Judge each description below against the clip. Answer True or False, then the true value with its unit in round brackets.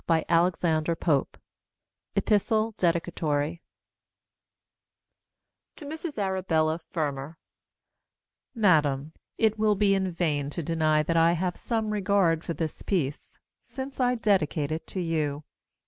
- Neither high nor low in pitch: True (170 Hz)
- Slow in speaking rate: True (110 wpm)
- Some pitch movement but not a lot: True (4.8 semitones)